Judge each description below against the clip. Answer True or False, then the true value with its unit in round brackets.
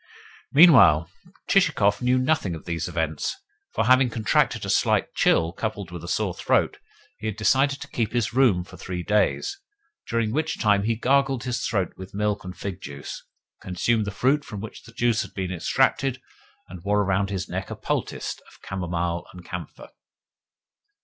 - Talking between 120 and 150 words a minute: False (175 wpm)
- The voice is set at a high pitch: False (105 Hz)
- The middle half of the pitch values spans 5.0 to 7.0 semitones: True (5.3 semitones)